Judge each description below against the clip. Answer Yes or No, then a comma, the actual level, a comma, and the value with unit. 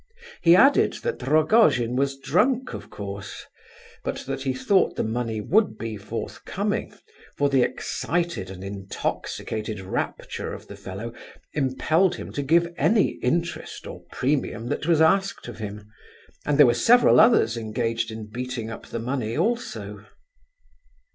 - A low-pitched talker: Yes, low, 130 Hz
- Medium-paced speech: Yes, average, 145 wpm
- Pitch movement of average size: No, wide, 7.3 semitones